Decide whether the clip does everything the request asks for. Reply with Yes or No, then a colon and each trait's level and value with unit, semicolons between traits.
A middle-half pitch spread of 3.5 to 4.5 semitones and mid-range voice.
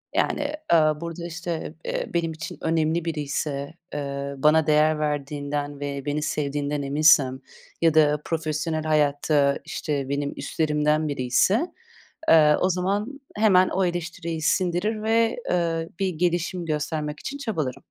No: average, 2.8 semitones; medium, 155 Hz